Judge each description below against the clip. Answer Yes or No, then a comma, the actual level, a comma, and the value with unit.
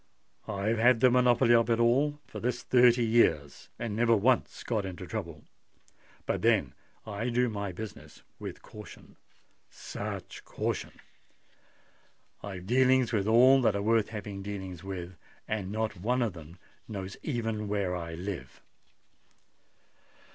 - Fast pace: No, slow, 135 wpm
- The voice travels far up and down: No, average, 3.6 semitones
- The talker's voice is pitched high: No, low, 110 Hz